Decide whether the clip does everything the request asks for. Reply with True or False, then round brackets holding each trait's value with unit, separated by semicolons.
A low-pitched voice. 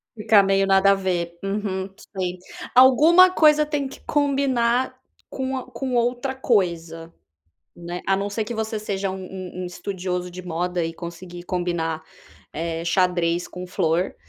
False (190 Hz)